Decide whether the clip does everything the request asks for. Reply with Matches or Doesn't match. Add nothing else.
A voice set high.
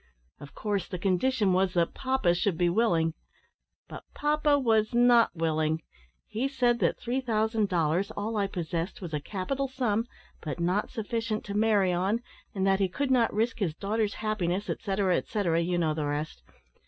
Matches